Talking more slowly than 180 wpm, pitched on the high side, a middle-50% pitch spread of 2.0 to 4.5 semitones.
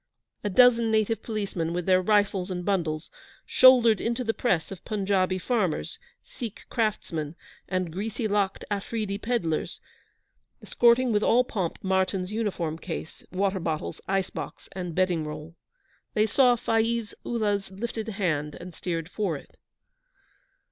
Yes: slow, 135 wpm; high, 195 Hz; average, 3.9 semitones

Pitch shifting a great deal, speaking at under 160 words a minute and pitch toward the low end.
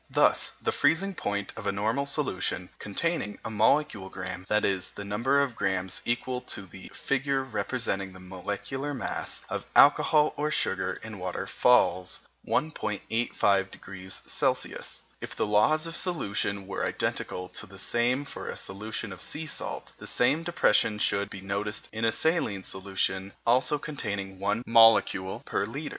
Yes: wide, 6.0 semitones; average, 150 wpm; low, 105 Hz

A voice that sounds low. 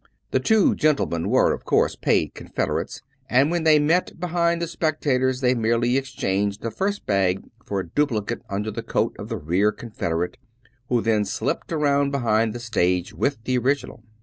Yes: low, 125 Hz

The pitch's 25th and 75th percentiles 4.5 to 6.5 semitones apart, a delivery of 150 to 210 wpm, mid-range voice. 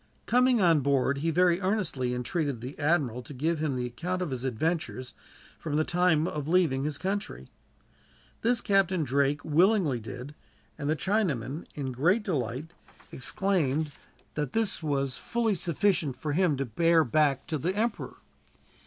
Yes: average, 5.0 semitones; average, 155 wpm; medium, 155 Hz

